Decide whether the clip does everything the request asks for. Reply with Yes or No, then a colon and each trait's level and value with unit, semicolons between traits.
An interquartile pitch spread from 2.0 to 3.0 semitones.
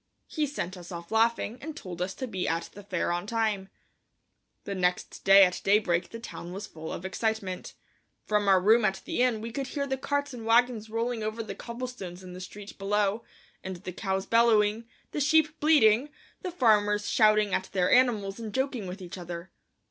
No: average, 3.8 semitones